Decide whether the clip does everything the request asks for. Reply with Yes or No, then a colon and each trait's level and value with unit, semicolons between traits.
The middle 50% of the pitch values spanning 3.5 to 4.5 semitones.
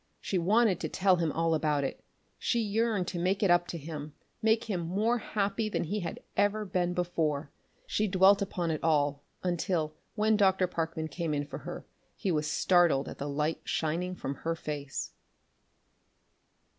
Yes: average, 4.2 semitones